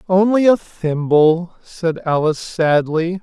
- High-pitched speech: No, medium, 170 Hz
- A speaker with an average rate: No, slow, 110 wpm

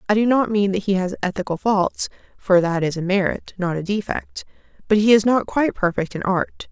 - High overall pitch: Yes, high, 195 Hz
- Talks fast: Yes, fast, 225 wpm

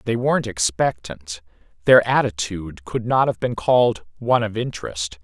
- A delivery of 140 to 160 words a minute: Yes, average, 150 wpm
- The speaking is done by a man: Yes, male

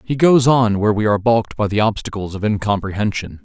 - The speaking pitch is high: No, low, 110 Hz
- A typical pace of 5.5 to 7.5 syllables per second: Yes, 6.3 syllables/s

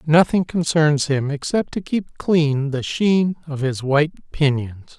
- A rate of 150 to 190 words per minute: Yes, average, 155 wpm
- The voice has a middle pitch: Yes, medium, 150 Hz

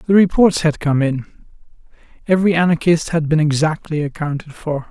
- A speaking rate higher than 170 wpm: No, average, 145 wpm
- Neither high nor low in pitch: Yes, medium, 160 Hz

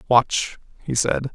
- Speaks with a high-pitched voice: No, low, 125 Hz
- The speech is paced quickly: No, slow, 135 wpm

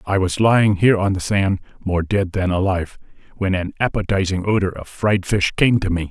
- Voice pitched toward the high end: No, very low, 95 Hz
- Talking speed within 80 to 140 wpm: No, fast, 205 wpm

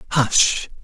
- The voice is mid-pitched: No, low, 130 Hz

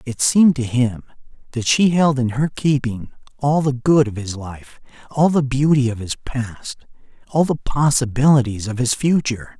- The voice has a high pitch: No, low, 130 Hz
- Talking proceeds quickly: No, average, 175 wpm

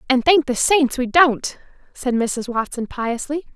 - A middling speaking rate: Yes, average, 170 wpm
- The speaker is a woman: Yes, female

